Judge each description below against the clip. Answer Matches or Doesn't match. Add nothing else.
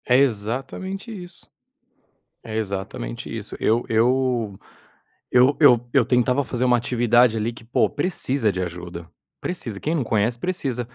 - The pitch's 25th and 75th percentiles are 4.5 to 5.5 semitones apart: Doesn't match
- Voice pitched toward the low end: Matches